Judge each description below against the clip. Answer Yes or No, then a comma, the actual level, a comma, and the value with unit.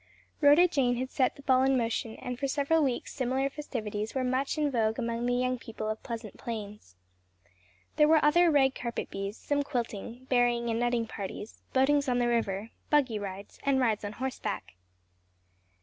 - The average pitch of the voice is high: Yes, high, 245 Hz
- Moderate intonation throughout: Yes, average, 3.3 semitones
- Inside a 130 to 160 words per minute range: No, average, 180 wpm